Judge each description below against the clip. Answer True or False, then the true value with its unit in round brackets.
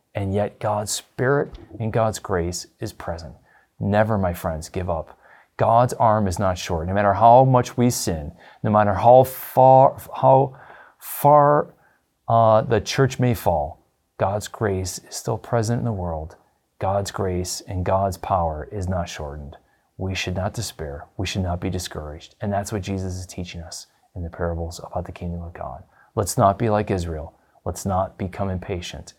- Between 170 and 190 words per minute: True (175 wpm)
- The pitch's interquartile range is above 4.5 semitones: False (3.8 semitones)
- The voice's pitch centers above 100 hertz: False (95 Hz)